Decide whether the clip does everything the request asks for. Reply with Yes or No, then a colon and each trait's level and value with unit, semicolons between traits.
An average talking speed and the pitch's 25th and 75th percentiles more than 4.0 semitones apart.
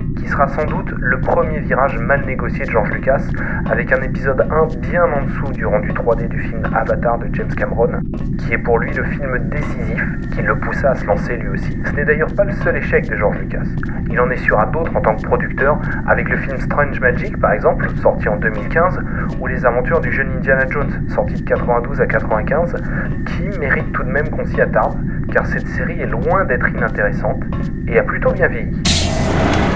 No: average, 210 wpm; average, 3.6 semitones